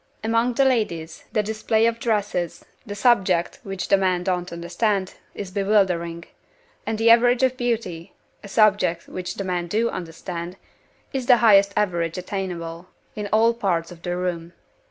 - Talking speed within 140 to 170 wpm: Yes, average, 155 wpm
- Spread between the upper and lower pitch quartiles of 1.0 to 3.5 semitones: No, average, 4.2 semitones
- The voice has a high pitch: Yes, high, 195 Hz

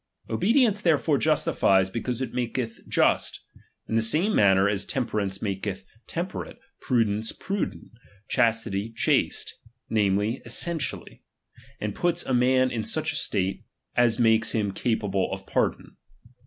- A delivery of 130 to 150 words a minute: Yes, slow, 135 wpm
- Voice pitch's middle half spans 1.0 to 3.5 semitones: No, average, 4.4 semitones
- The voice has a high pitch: No, low, 115 Hz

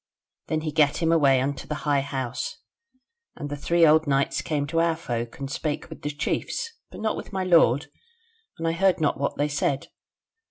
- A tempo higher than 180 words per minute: Yes, average, 200 wpm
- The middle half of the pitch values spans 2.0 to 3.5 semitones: Yes, average, 2.8 semitones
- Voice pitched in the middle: Yes, medium, 150 Hz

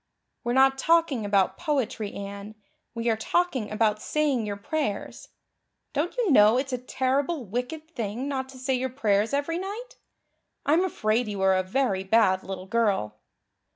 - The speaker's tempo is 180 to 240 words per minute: No, average, 160 wpm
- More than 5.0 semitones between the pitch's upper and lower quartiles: Yes, wide, 5.6 semitones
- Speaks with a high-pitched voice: Yes, high, 245 Hz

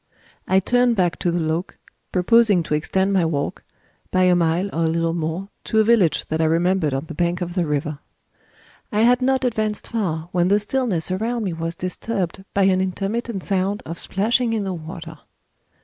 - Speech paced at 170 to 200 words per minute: Yes, average, 195 wpm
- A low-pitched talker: No, medium, 185 Hz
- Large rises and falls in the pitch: No, average, 4.1 semitones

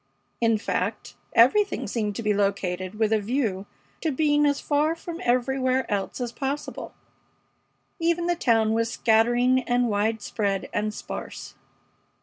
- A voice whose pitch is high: Yes, high, 235 Hz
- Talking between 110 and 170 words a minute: Yes, slow, 135 wpm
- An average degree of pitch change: Yes, average, 4.6 semitones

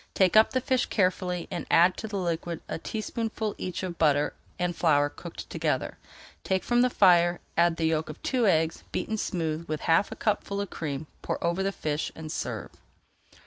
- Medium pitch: Yes, medium, 175 Hz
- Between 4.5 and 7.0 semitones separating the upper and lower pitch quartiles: No, average, 3.7 semitones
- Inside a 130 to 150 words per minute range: No, average, 190 wpm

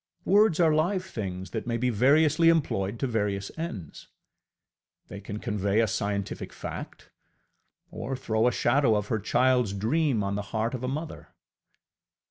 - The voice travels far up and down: Yes, wide, 5.9 semitones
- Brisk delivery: No, average, 155 wpm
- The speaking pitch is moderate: No, low, 115 Hz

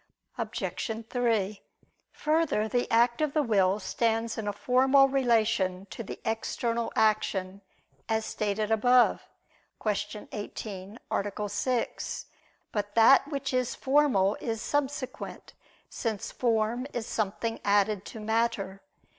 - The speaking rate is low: Yes, slow, 120 wpm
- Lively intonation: No, average, 3.1 semitones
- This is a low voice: No, high, 225 Hz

